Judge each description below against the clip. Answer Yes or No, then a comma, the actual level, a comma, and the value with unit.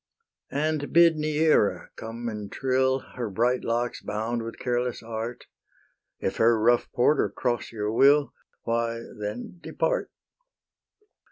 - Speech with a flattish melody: No, average, 3.2 semitones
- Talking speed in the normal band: No, slow, 120 wpm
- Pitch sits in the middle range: No, low, 120 Hz